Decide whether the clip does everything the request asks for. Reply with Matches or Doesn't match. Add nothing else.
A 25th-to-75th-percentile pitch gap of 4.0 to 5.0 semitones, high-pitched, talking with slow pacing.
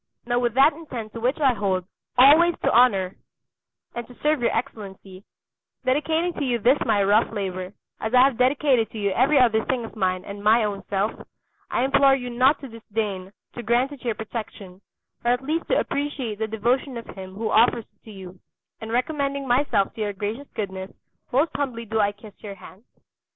Doesn't match